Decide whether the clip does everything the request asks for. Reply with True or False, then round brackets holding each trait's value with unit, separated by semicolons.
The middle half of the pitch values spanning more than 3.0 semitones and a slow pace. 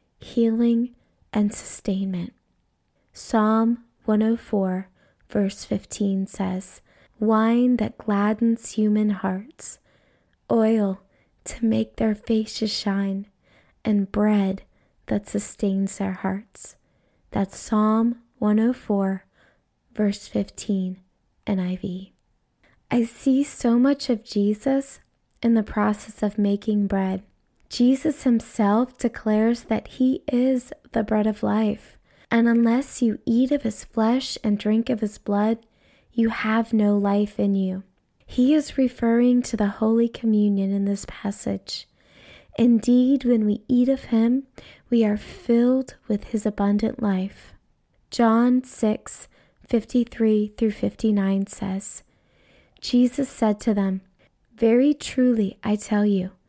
False (2.7 semitones; 115 wpm)